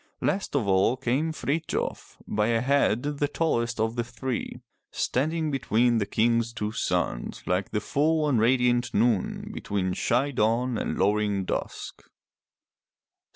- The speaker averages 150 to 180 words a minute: No, average, 140 wpm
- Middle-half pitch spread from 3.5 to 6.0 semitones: Yes, average, 4.6 semitones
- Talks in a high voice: No, low, 120 Hz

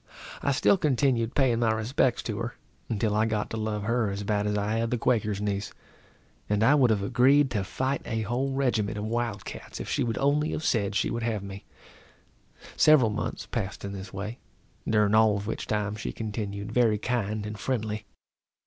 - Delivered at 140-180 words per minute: No, average, 200 wpm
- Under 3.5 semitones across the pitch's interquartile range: Yes, average, 2.7 semitones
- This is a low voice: Yes, low, 110 Hz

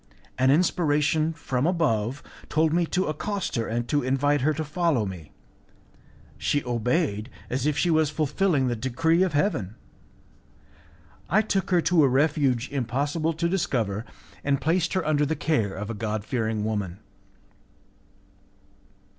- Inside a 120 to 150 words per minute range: Yes, average, 145 wpm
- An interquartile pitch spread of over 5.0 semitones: Yes, wide, 5.4 semitones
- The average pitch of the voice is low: No, medium, 145 Hz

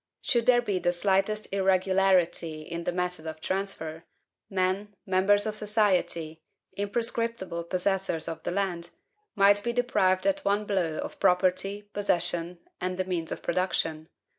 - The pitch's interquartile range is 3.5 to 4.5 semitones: No, average, 2.7 semitones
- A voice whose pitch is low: No, high, 190 Hz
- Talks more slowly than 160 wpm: Yes, average, 140 wpm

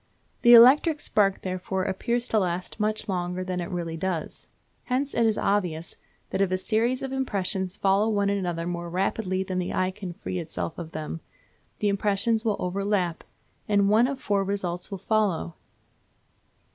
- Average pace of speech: Yes, average, 170 wpm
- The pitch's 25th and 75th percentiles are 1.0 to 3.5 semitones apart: Yes, average, 3.2 semitones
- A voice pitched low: No, high, 195 Hz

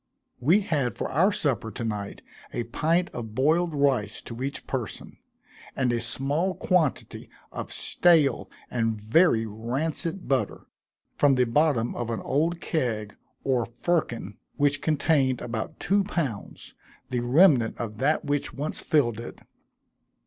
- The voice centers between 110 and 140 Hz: Yes, low, 135 Hz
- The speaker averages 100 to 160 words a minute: Yes, average, 140 wpm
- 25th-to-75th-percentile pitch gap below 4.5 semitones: No, average, 5.3 semitones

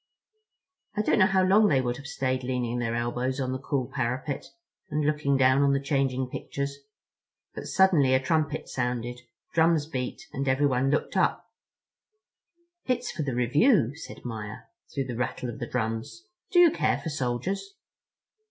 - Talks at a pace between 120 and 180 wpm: Yes, average, 165 wpm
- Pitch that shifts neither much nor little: Yes, average, 3.5 semitones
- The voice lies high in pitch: No, low, 135 Hz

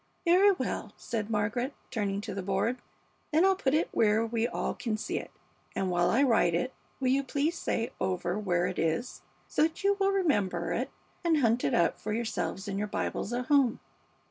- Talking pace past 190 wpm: Yes, average, 200 wpm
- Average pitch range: No, wide, 6.0 semitones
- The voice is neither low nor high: No, high, 230 Hz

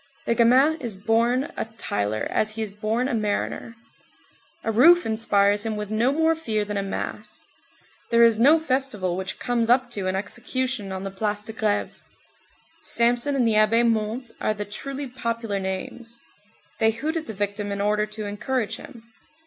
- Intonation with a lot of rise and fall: No, average, 3.0 semitones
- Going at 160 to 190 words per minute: Yes, average, 180 wpm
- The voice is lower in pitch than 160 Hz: No, high, 225 Hz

